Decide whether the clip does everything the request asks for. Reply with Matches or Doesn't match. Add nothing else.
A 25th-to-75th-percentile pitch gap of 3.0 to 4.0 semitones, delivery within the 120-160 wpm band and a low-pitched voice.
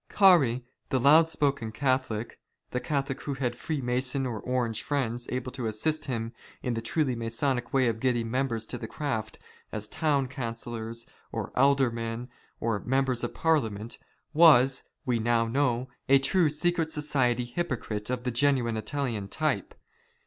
Matches